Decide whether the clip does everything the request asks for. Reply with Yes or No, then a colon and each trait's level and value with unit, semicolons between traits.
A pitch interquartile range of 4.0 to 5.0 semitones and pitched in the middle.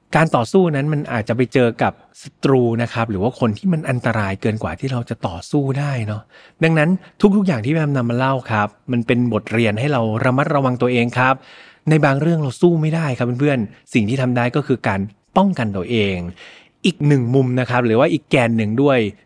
No: average, 4.3 semitones; low, 125 Hz